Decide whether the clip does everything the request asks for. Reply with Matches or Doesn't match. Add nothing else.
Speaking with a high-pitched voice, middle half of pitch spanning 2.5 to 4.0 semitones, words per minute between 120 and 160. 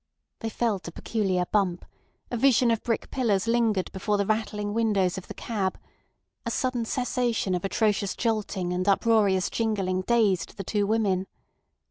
Matches